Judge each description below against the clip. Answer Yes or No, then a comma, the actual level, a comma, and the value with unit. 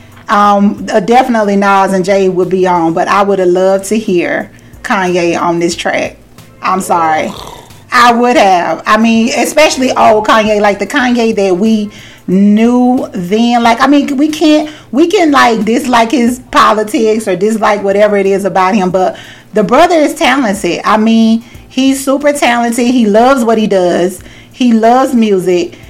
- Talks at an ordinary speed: Yes, average, 170 wpm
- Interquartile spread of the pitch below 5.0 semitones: Yes, average, 4.2 semitones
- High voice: Yes, high, 220 Hz